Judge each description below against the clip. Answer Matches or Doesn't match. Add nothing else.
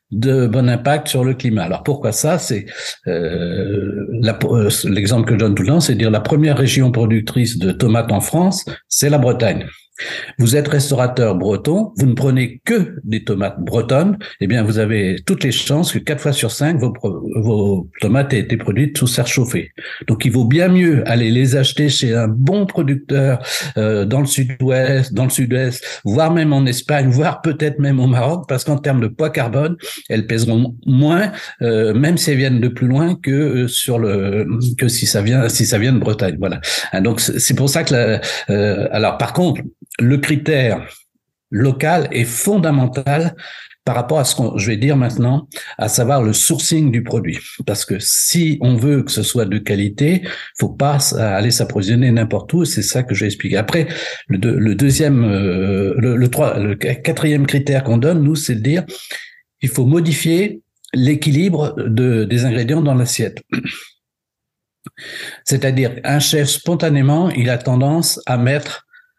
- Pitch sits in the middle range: Doesn't match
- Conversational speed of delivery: Matches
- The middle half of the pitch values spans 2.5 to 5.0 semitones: Matches